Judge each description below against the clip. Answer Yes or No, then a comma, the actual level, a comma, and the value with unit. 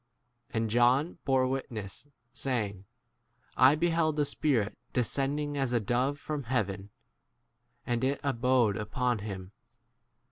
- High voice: No, low, 125 Hz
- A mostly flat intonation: No, average, 4.2 semitones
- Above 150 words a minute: No, slow, 135 wpm